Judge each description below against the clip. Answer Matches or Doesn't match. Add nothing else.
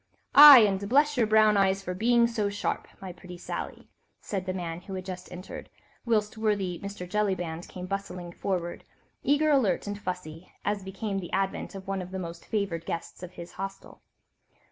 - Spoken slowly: Doesn't match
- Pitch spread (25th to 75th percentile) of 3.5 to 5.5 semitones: Doesn't match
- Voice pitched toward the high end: Matches